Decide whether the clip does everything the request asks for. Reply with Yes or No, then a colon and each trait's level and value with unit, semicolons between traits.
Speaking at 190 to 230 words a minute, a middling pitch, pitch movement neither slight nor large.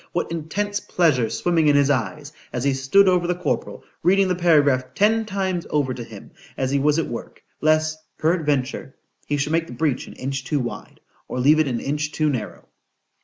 Yes: average, 195 wpm; medium, 150 Hz; average, 4.4 semitones